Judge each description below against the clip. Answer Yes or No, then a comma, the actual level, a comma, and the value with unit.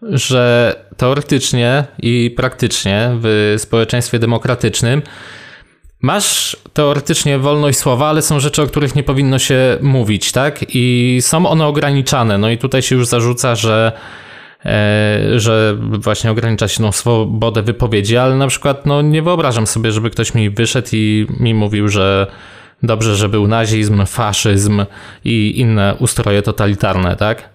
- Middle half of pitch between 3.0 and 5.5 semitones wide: Yes, average, 3.8 semitones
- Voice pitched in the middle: No, low, 115 Hz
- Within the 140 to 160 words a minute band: Yes, average, 145 wpm